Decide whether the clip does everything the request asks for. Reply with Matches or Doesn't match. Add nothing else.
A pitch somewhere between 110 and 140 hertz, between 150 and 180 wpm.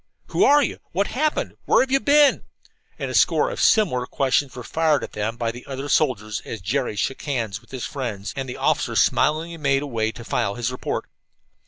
Doesn't match